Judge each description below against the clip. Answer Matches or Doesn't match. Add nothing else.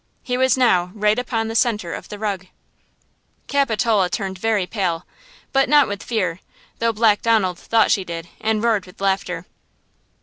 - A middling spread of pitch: Matches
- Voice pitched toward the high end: Matches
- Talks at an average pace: Matches